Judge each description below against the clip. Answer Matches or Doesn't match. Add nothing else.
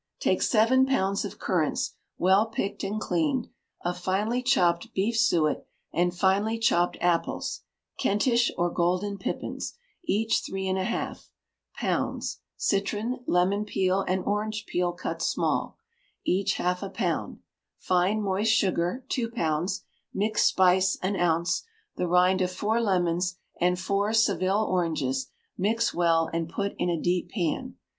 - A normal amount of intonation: Matches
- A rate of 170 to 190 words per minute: Doesn't match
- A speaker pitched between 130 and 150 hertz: Doesn't match